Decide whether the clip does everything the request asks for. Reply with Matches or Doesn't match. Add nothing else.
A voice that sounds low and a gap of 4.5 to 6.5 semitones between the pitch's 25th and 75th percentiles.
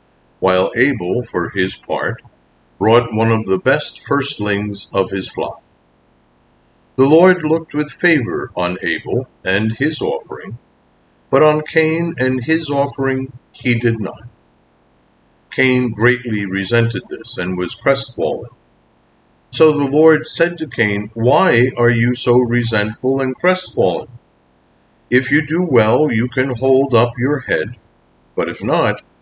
Matches